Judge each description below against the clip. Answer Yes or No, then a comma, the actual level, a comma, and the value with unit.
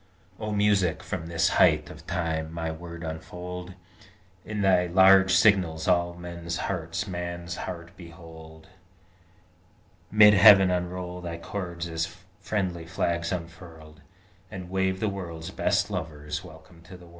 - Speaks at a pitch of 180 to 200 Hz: No, very low, 85 Hz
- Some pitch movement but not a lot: No, narrow, 2.3 semitones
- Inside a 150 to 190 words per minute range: No, slow, 135 wpm